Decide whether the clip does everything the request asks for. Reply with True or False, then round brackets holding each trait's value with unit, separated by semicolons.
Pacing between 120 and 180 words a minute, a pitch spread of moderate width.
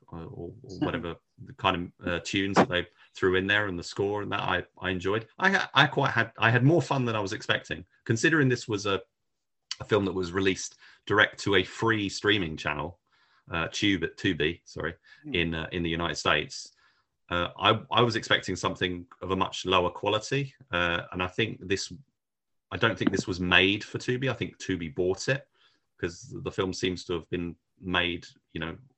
False (205 wpm; 4.5 semitones)